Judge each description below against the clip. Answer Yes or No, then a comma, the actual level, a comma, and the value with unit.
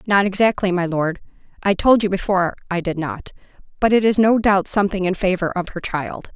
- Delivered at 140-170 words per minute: No, average, 200 wpm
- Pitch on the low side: No, high, 190 Hz